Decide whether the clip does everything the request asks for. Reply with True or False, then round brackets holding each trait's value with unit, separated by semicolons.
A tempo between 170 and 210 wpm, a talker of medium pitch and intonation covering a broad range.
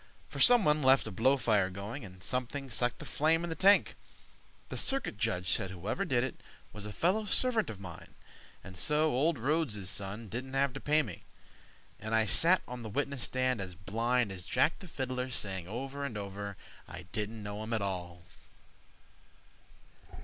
False (180 wpm; 120 Hz; 5.9 semitones)